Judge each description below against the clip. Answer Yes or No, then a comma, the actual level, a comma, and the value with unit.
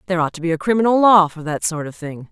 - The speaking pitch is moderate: Yes, medium, 175 Hz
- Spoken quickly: Yes, fast, 310 wpm